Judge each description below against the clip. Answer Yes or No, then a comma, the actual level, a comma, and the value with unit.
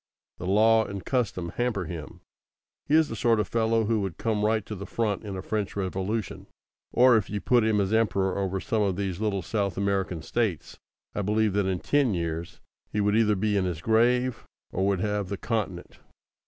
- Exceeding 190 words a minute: Yes, fast, 205 wpm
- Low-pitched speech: Yes, low, 105 Hz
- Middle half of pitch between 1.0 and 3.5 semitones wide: Yes, average, 2.8 semitones